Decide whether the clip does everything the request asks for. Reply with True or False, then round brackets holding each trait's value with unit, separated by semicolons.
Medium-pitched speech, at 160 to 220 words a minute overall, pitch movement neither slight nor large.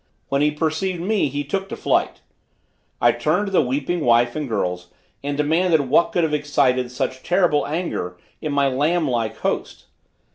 True (145 Hz; 175 wpm; 4.7 semitones)